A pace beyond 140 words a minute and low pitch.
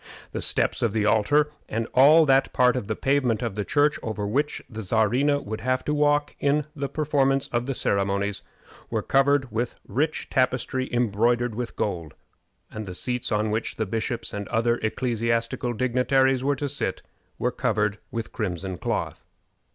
Yes: average, 170 wpm; low, 120 Hz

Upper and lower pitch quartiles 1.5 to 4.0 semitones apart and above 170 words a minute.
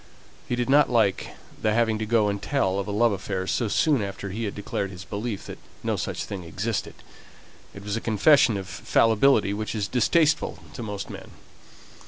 Yes: average, 2.9 semitones; average, 195 wpm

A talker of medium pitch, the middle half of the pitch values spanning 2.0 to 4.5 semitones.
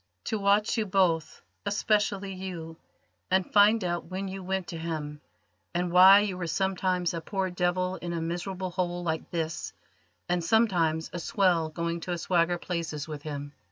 Yes: medium, 180 Hz; narrow, 2.4 semitones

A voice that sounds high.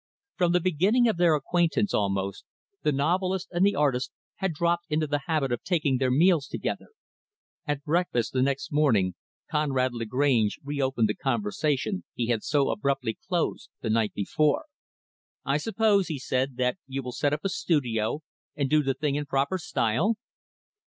No: medium, 145 Hz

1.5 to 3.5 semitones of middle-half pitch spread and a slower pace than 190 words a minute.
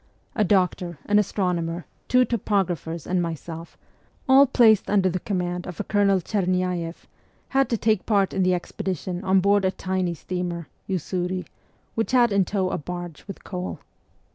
Yes: narrow, 2.5 semitones; average, 165 wpm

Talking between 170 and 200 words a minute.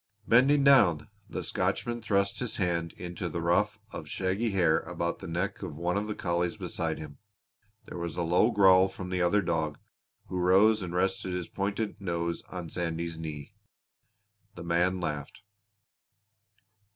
No: average, 160 wpm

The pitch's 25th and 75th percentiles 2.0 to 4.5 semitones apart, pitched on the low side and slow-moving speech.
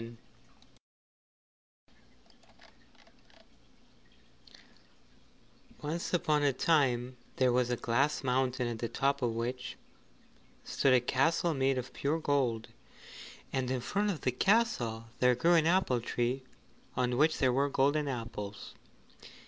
Yes: average, 3.3 semitones; low, 130 Hz; slow, 115 wpm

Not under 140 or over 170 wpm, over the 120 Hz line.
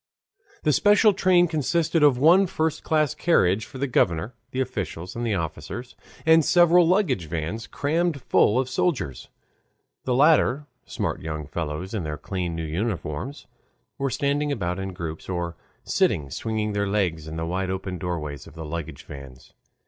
No: average, 160 wpm; low, 105 Hz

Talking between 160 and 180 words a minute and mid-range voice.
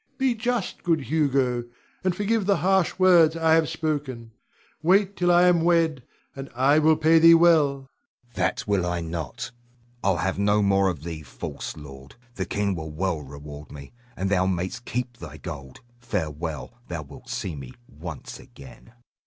No: average, 170 wpm; low, 120 Hz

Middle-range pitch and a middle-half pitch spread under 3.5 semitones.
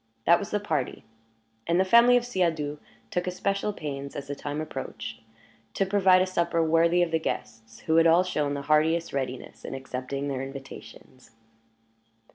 No: medium, 160 Hz; average, 4.8 semitones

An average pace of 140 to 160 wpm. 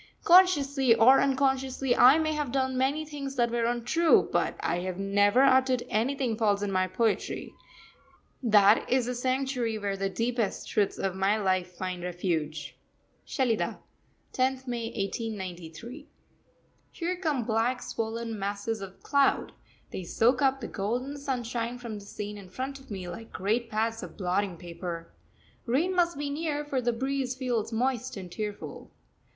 Yes: average, 155 wpm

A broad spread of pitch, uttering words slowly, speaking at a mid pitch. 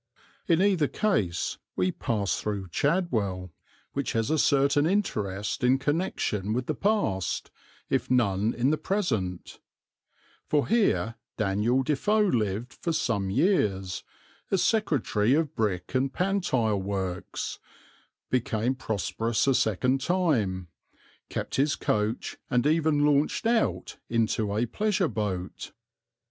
No: wide, 7.4 semitones; slow, 120 wpm; low, 125 Hz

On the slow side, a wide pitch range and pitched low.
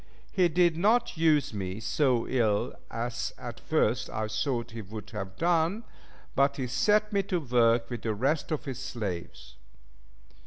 No: average, 160 wpm; wide, 7.0 semitones; low, 125 Hz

